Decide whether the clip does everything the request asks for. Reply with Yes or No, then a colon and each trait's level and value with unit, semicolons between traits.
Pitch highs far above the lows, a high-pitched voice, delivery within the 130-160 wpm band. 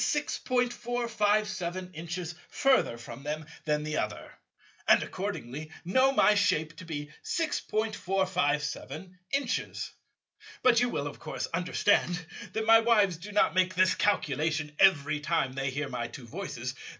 No: wide, 6.1 semitones; medium, 180 Hz; slow, 135 wpm